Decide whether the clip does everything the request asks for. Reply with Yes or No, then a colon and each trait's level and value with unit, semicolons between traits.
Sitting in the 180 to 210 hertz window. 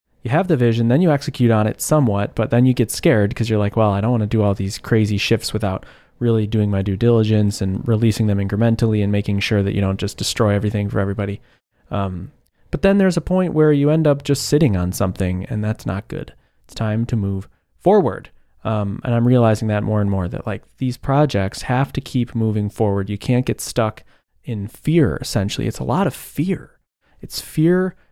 No: low, 110 Hz